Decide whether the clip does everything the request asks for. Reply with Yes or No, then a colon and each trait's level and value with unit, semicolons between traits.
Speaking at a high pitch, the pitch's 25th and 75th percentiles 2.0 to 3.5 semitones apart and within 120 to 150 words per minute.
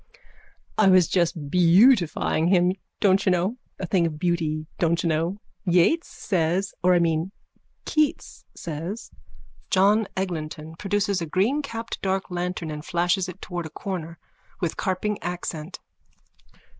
No: medium, 180 Hz; average, 2.8 semitones; average, 140 wpm